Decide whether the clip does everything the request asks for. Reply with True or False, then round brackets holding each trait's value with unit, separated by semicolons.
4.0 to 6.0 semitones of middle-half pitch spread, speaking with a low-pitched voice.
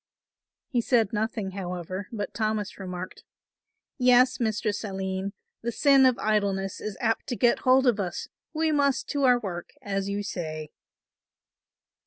False (4.3 semitones; 215 Hz)